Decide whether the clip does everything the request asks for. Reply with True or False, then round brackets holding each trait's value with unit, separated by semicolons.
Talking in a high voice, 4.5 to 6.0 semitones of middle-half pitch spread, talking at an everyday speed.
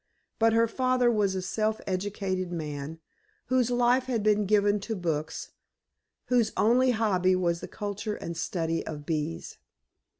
True (205 Hz; 4.8 semitones; 145 wpm)